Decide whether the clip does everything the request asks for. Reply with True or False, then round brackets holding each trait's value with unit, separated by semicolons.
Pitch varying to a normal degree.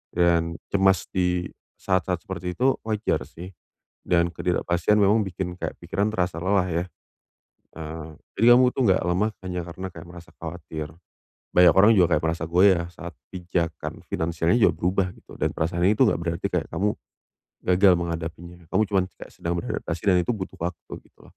False (2.2 semitones)